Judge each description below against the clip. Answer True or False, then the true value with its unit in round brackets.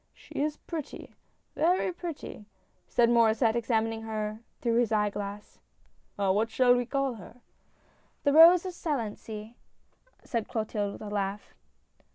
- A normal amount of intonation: True (4.5 semitones)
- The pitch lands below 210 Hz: False (230 Hz)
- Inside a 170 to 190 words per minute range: False (160 wpm)